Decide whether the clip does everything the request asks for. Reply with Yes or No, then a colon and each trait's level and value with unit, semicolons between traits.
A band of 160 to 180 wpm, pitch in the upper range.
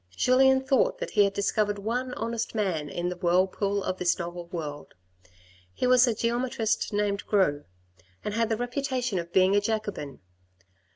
Yes: average, 165 wpm; high, 205 Hz